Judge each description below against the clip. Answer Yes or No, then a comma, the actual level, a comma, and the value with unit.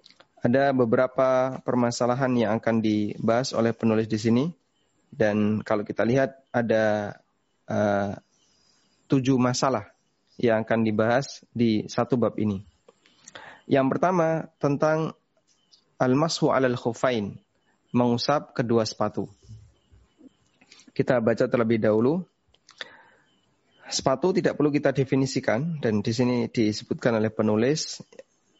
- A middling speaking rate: Yes, average, 105 wpm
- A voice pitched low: Yes, low, 120 Hz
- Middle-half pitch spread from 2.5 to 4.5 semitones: Yes, average, 3.7 semitones